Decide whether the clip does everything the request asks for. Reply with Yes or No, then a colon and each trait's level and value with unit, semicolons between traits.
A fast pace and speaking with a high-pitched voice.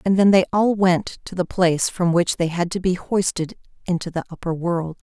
No: fast, 225 wpm; medium, 180 Hz